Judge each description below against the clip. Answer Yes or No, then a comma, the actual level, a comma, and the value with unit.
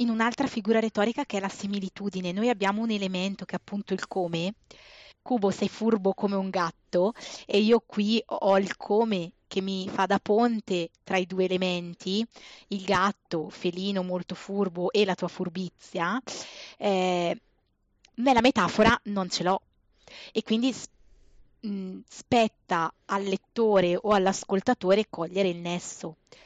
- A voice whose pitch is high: Yes, high, 195 Hz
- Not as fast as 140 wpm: No, average, 145 wpm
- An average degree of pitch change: Yes, average, 3.0 semitones